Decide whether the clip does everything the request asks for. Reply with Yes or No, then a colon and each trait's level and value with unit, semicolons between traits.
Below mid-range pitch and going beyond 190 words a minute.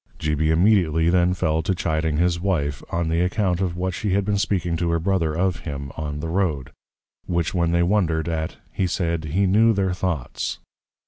Yes: very low, 85 Hz; average, 200 wpm